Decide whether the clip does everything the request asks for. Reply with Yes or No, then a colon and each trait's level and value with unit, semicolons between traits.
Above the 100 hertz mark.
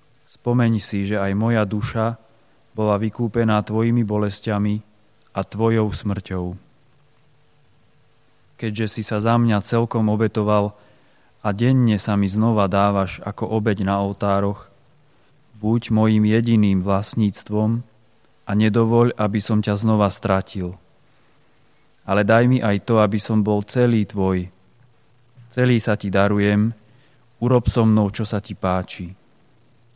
Yes: low, 110 Hz